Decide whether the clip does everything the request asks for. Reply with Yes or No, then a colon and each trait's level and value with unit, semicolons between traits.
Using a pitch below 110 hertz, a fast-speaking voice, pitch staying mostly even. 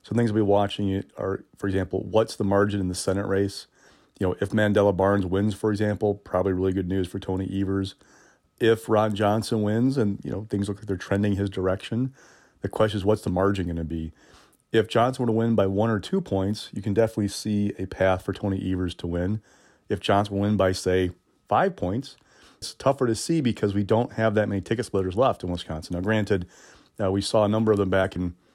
Yes: low, 100 Hz; fast, 230 wpm; narrow, 2.3 semitones